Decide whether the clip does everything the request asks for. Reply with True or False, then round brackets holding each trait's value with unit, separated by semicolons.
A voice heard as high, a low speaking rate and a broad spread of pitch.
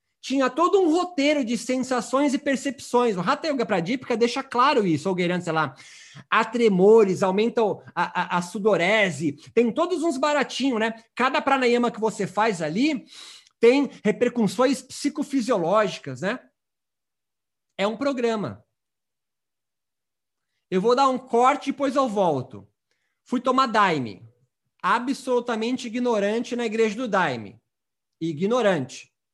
False (230 Hz; 130 wpm; 6.0 semitones)